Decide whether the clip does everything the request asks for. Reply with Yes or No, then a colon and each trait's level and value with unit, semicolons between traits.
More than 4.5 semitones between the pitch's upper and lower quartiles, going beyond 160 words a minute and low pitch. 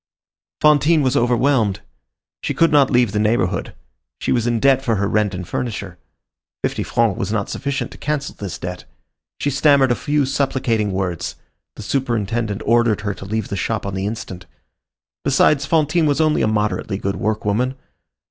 Yes: average, 5.2 semitones; average, 170 wpm; low, 115 Hz